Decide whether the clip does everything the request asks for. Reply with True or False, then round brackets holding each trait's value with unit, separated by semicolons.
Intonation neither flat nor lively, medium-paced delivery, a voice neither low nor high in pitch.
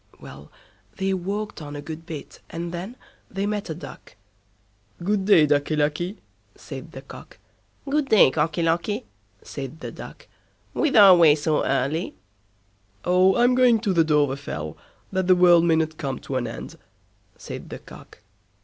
True (4.6 semitones; 155 wpm; 170 Hz)